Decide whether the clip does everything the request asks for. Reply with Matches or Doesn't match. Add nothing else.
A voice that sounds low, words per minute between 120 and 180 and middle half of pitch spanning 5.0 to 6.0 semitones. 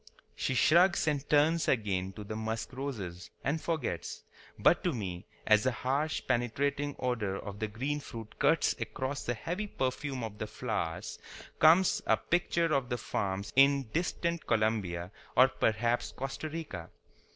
Matches